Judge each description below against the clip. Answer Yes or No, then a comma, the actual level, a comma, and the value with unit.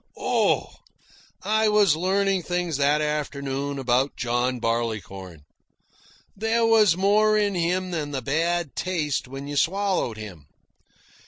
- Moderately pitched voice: Yes, medium, 150 Hz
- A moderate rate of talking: No, slow, 120 wpm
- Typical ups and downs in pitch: No, wide, 6.6 semitones